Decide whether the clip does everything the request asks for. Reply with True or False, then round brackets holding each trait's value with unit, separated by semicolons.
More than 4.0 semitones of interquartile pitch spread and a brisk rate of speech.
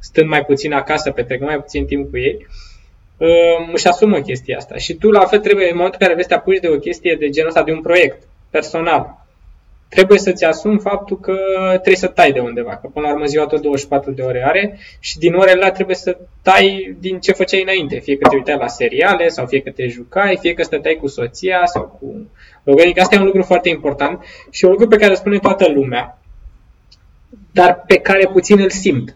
True (5.3 semitones; 220 wpm)